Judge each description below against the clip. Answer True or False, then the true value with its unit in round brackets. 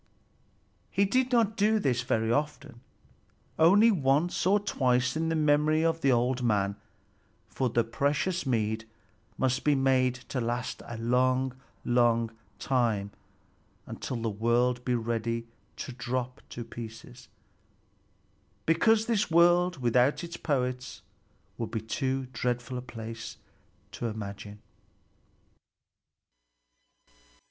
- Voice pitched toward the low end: True (125 Hz)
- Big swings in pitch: False (4.6 semitones)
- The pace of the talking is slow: True (115 wpm)